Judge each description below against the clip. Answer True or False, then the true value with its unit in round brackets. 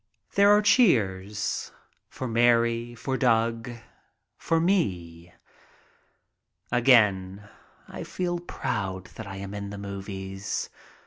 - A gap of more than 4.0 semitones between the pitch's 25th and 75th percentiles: True (4.5 semitones)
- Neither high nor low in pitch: False (110 Hz)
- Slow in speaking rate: True (110 wpm)